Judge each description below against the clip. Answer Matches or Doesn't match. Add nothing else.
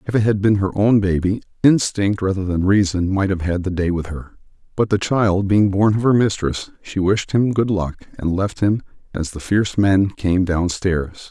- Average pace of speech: Doesn't match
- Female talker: Doesn't match